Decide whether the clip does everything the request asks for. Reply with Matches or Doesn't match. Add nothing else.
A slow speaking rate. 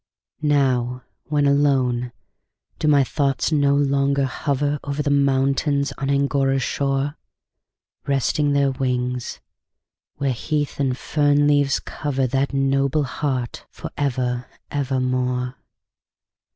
Matches